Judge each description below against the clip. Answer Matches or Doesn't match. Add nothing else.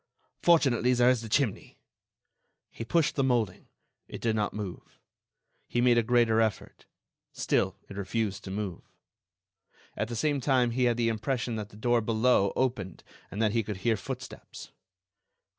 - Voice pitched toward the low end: Matches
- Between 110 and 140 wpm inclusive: Doesn't match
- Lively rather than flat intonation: Doesn't match